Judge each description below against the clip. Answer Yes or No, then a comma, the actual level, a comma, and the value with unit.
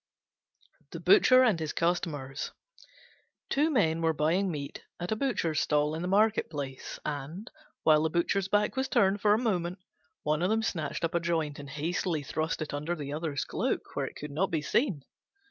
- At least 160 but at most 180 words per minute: No, average, 190 wpm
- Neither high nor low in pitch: Yes, medium, 165 Hz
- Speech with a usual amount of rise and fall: Yes, average, 4.7 semitones